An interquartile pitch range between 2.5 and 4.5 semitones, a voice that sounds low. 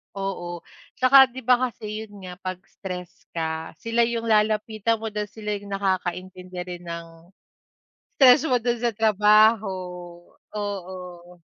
No: average, 3.7 semitones; high, 205 Hz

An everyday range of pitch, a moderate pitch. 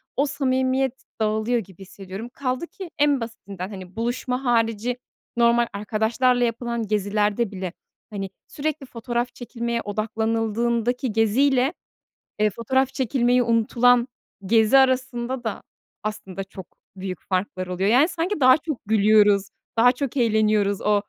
No: average, 3.4 semitones; high, 230 Hz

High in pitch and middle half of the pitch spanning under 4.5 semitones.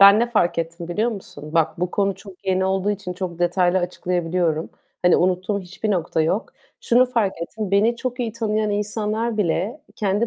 Yes: high, 195 Hz; average, 3.3 semitones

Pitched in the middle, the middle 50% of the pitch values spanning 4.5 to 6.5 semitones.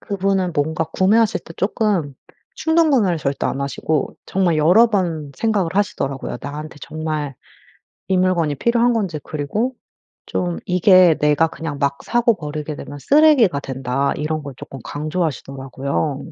Yes: medium, 160 Hz; average, 5.3 semitones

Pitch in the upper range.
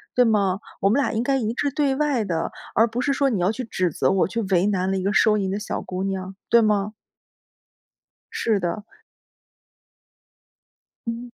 Yes: high, 210 Hz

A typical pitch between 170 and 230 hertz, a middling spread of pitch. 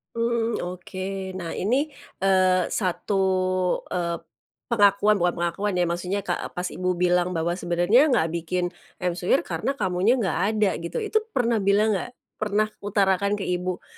Yes: high, 190 Hz; average, 3.0 semitones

